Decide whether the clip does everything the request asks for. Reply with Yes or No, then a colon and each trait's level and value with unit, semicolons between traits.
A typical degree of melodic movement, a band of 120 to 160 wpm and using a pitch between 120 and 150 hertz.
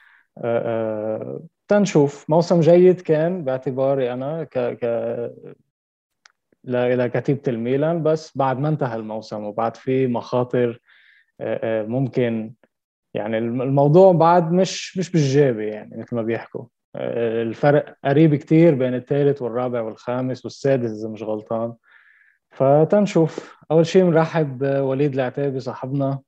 No: average, 4.9 semitones; average, 110 wpm; low, 135 Hz